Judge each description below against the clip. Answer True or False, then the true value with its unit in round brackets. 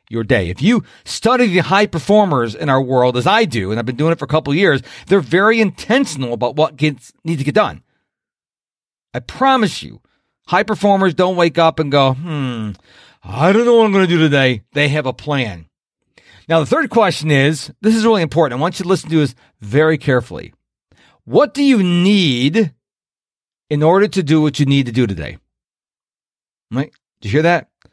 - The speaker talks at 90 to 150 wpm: False (205 wpm)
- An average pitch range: False (6.6 semitones)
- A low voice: False (155 Hz)